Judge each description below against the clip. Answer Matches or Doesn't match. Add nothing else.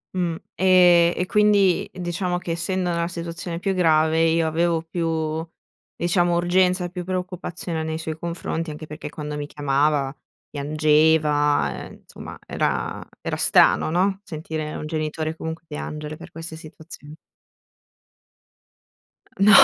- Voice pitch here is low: Doesn't match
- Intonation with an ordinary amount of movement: Doesn't match